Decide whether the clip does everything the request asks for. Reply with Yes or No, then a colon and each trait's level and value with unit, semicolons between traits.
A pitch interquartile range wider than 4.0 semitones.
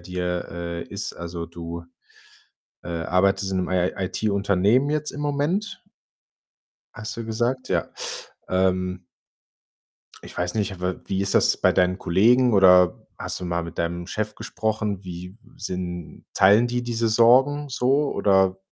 Yes: average, 4.5 semitones